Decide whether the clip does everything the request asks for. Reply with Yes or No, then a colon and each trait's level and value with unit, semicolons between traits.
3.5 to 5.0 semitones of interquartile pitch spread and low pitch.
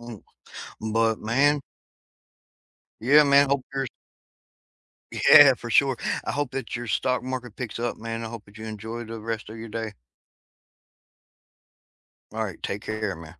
No: average, 3.0 semitones; low, 115 Hz